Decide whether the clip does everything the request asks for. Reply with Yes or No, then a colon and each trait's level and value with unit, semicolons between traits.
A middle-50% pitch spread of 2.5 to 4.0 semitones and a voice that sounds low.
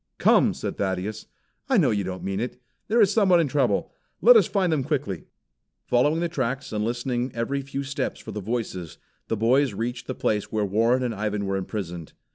No: average, 5.1 semitones; low, 120 Hz